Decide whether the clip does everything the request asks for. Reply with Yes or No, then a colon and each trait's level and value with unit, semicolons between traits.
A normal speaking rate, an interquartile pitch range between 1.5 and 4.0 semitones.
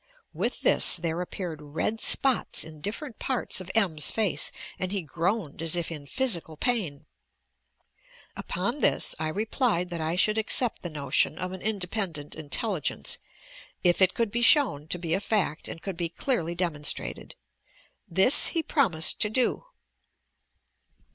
No: average, 155 wpm; average, 5.3 semitones